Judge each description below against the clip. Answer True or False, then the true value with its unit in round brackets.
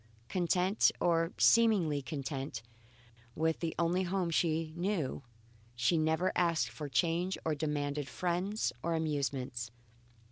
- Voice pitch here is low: False (160 Hz)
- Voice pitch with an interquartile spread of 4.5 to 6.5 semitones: False (3.4 semitones)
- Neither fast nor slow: False (115 wpm)